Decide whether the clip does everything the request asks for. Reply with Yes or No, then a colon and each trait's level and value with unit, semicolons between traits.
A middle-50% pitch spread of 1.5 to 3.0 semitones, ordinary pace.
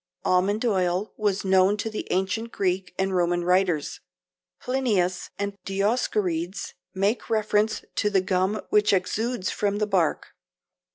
No: narrow, 2.4 semitones; slow, 130 wpm